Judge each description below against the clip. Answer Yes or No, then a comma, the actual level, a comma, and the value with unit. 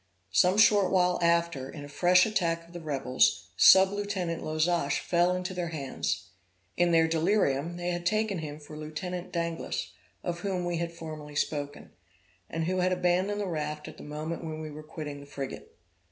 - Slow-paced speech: No, average, 180 wpm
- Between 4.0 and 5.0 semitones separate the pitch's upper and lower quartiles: No, average, 2.9 semitones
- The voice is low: No, medium, 170 Hz